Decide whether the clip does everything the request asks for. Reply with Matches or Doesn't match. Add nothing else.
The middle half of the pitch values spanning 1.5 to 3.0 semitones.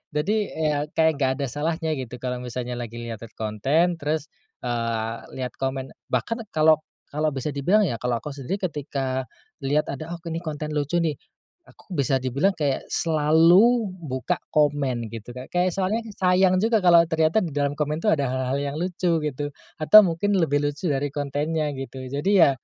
Doesn't match